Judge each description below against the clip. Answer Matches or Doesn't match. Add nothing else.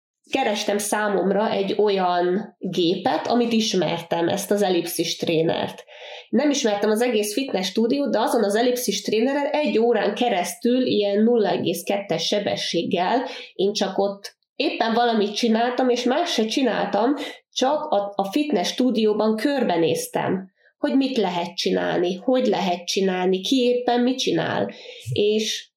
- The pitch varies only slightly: Doesn't match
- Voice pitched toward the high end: Matches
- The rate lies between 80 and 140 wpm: Matches